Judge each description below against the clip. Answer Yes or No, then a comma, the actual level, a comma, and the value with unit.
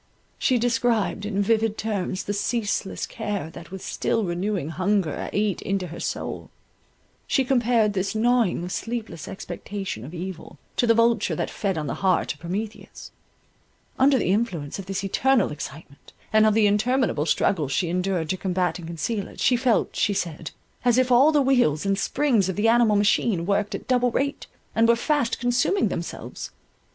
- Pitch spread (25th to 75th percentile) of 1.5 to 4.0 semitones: No, average, 4.5 semitones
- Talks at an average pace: Yes, average, 175 wpm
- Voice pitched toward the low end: No, high, 205 Hz